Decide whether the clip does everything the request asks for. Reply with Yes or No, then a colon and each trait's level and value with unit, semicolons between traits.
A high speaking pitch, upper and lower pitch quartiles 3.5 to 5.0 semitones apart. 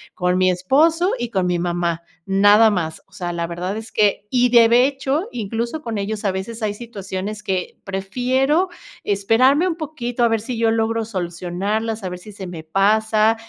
Yes: high, 215 Hz; average, 4.2 semitones